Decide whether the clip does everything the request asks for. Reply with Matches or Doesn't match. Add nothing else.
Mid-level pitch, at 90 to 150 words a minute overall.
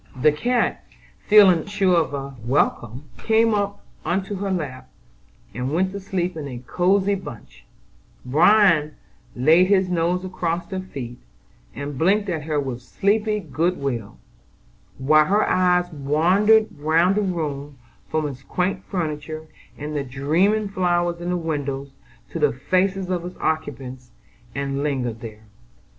Matches